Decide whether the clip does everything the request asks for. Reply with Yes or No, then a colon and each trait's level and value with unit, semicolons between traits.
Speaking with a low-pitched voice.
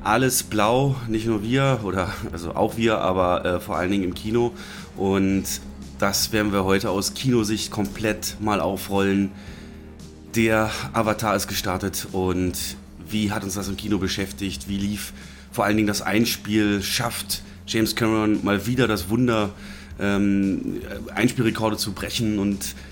Yes: low, 100 Hz